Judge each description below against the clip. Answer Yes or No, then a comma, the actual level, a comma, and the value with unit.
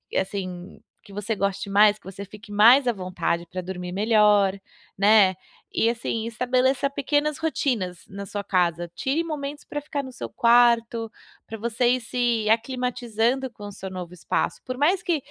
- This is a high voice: Yes, high, 225 Hz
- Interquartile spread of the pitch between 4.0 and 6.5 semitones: Yes, average, 4.4 semitones